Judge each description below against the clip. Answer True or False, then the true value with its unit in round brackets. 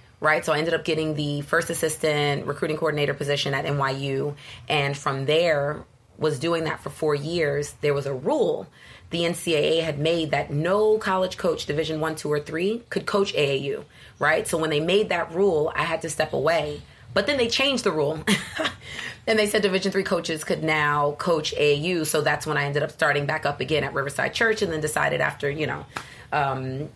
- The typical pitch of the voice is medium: True (155 Hz)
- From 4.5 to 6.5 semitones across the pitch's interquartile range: False (2.6 semitones)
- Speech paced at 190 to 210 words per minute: True (205 wpm)